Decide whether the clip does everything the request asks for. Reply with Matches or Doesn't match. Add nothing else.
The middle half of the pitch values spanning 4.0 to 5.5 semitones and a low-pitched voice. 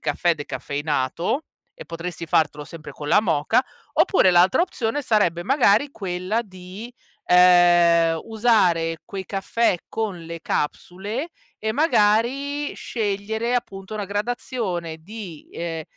Doesn't match